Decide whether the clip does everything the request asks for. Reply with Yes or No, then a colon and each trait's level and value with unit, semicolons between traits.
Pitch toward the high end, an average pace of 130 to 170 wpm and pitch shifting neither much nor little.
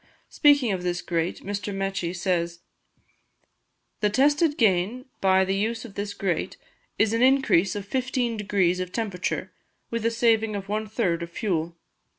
Yes: high, 200 Hz; average, 160 wpm; average, 4.1 semitones